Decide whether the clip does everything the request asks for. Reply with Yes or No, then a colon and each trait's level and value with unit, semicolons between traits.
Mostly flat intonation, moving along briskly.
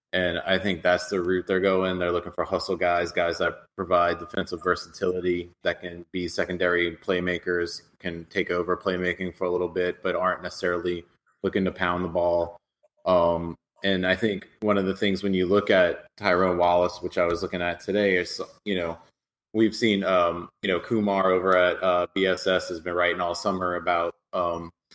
No: narrow, 1.3 semitones; average, 190 wpm